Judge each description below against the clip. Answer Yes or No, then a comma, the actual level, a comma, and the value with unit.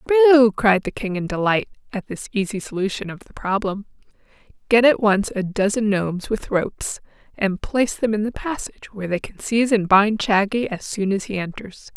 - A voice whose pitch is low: No, high, 210 Hz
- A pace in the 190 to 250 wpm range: Yes, average, 195 wpm